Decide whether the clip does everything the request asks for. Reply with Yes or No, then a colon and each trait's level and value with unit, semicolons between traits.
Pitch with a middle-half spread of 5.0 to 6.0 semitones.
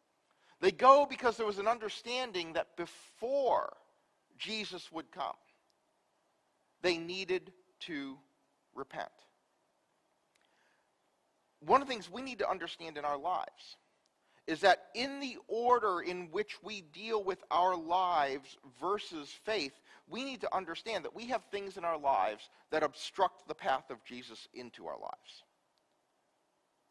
Yes: wide, 5.5 semitones